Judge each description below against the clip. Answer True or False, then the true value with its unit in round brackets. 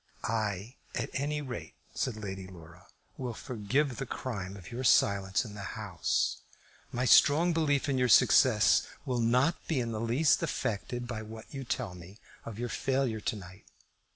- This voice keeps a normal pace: True (170 wpm)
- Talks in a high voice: False (115 Hz)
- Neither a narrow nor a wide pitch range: True (4.4 semitones)